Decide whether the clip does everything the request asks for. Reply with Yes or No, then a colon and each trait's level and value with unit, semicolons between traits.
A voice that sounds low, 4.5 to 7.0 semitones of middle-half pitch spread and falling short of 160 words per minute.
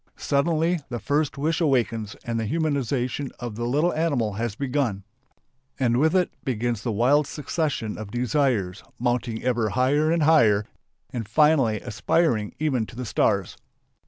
Yes: low, 125 Hz; average, 4.8 semitones; average, 150 wpm